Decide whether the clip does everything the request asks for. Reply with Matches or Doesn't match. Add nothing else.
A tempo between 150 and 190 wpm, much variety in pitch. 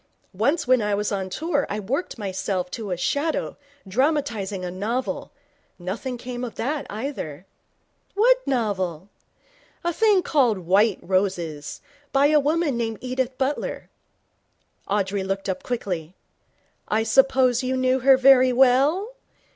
Doesn't match